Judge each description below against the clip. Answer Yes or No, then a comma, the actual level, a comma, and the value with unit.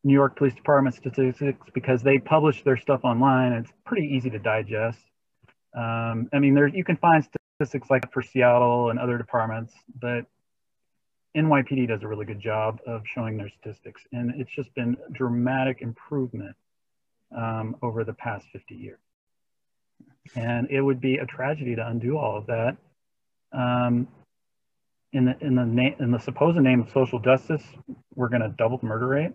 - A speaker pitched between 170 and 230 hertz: No, low, 125 Hz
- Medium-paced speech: Yes, average, 175 wpm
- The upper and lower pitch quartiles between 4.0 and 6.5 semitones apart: No, average, 2.7 semitones